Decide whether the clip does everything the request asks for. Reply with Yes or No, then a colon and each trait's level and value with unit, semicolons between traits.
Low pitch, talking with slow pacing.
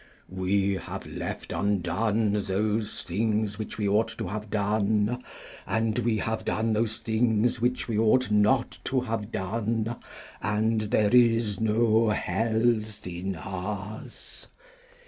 Yes: low, 110 Hz; slow, 125 wpm